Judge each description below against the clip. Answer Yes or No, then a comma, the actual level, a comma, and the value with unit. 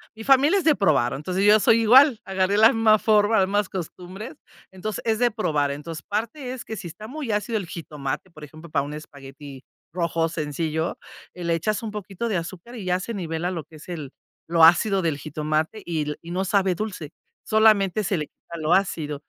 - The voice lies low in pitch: No, medium, 185 Hz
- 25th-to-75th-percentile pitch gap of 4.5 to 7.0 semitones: Yes, average, 5.3 semitones